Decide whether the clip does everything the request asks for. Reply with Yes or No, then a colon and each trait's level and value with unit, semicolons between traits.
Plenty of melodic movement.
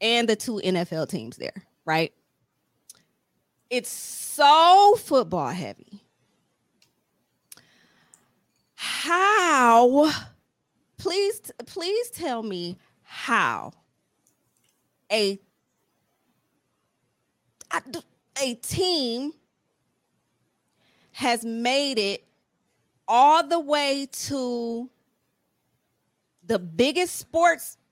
Yes: wide, 7.7 semitones